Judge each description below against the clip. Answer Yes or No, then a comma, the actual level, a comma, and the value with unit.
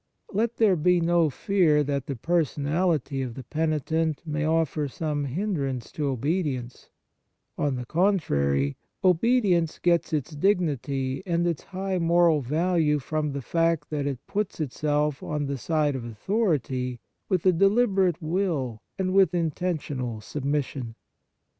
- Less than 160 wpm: Yes, average, 140 wpm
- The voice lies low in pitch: No, medium, 155 Hz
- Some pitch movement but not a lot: Yes, average, 4.2 semitones